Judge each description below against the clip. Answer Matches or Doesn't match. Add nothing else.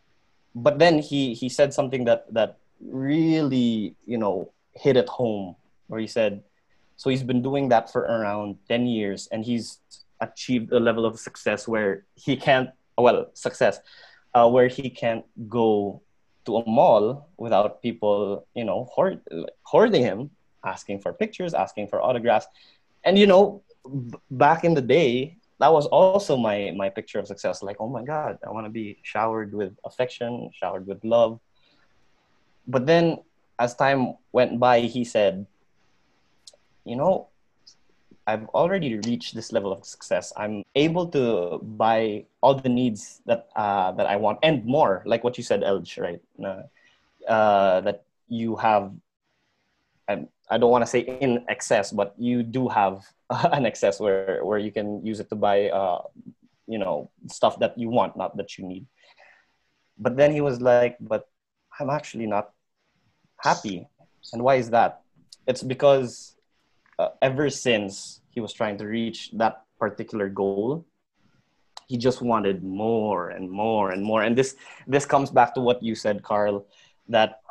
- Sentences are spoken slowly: Doesn't match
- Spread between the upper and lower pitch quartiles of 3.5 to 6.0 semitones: Matches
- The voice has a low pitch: Matches